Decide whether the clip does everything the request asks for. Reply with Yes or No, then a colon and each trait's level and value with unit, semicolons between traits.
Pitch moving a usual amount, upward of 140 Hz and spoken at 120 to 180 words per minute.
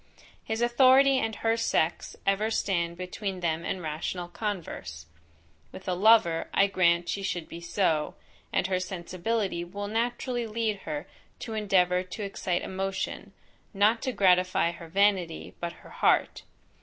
Yes: average, 3.9 semitones; high, 190 Hz; average, 145 wpm